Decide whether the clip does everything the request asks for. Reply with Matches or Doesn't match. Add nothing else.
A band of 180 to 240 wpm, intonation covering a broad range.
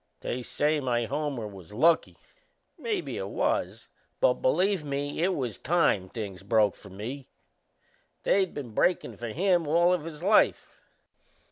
Doesn't match